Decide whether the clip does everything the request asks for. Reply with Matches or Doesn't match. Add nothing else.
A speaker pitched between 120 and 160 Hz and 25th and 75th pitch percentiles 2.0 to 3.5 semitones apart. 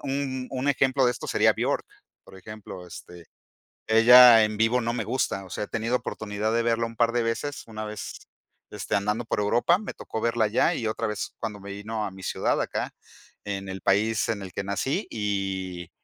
Doesn't match